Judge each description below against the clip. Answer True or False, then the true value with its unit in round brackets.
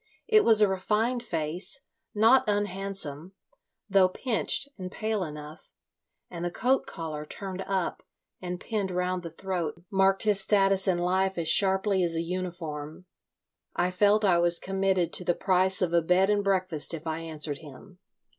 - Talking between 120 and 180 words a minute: True (165 wpm)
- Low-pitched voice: False (185 Hz)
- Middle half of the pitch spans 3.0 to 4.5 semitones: False (2.6 semitones)